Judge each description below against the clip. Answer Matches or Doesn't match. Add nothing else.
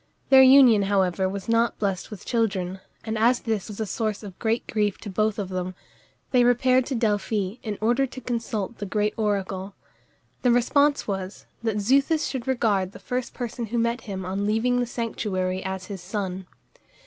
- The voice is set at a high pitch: Matches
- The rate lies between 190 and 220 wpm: Doesn't match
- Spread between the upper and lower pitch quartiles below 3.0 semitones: Doesn't match